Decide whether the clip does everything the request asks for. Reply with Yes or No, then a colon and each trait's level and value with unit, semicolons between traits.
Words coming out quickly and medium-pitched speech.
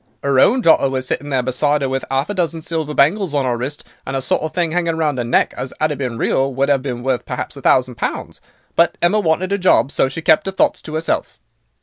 Yes: fast, 260 wpm; medium, 145 Hz